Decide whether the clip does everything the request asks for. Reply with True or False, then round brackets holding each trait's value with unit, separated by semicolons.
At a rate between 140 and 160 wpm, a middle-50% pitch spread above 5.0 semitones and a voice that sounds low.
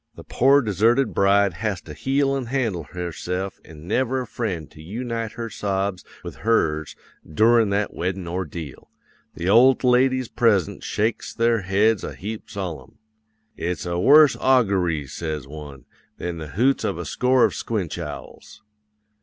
True (155 wpm; 5.4 semitones; 100 Hz)